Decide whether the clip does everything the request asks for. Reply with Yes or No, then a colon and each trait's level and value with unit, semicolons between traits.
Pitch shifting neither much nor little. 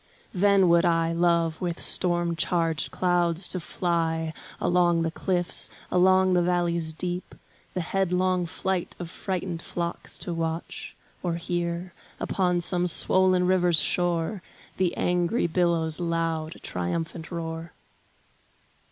No: narrow, 1.4 semitones